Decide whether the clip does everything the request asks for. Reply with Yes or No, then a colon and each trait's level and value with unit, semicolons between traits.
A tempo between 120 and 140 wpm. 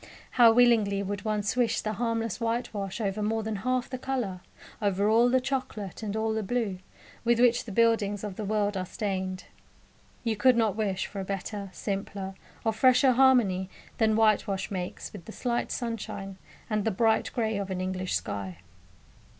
No: average, 175 wpm